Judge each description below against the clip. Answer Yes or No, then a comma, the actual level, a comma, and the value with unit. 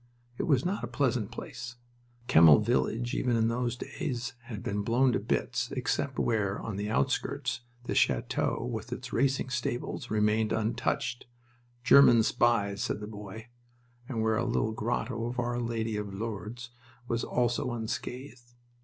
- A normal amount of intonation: No, narrow, 2.2 semitones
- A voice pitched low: Yes, low, 115 Hz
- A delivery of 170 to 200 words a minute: No, average, 155 wpm